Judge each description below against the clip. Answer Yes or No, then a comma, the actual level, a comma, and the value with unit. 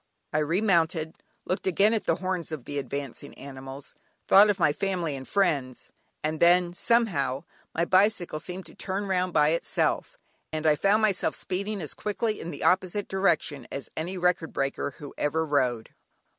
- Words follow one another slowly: No, average, 170 wpm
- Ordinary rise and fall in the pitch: Yes, average, 4.7 semitones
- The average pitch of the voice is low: No, medium, 170 Hz